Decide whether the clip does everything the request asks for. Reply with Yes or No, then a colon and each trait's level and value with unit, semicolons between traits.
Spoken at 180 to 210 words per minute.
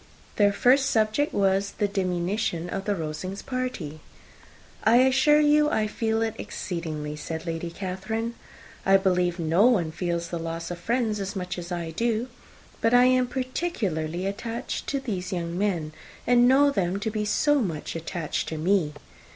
No: average, 160 wpm